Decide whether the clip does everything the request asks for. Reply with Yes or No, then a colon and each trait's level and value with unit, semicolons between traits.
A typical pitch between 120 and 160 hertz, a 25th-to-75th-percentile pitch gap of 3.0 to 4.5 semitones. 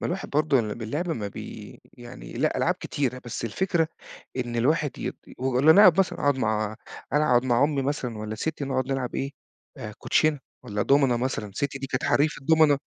Yes: low, 135 Hz; average, 3.8 semitones